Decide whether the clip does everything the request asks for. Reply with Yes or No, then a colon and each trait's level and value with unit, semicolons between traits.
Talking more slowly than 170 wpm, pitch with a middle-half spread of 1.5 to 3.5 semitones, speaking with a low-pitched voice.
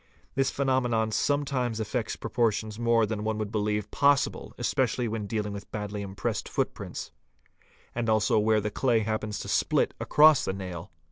Yes: average, 155 wpm; narrow, 2.5 semitones; low, 110 Hz